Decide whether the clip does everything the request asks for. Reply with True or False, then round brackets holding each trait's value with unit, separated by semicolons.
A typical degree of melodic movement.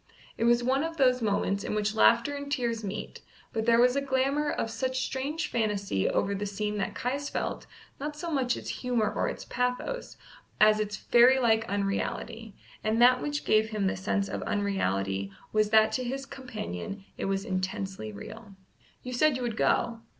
True (4.1 semitones)